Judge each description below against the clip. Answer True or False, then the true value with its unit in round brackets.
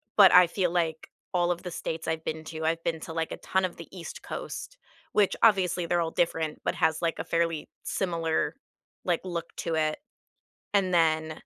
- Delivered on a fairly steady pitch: True (1.8 semitones)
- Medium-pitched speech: True (170 Hz)